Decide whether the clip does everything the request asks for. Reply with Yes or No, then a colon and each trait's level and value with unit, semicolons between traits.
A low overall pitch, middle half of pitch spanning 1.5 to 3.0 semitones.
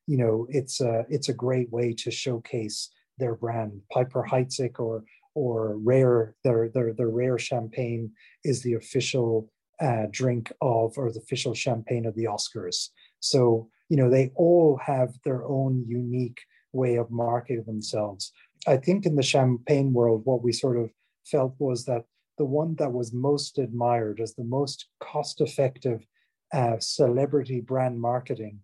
Yes: low, 125 Hz; narrow, 2.5 semitones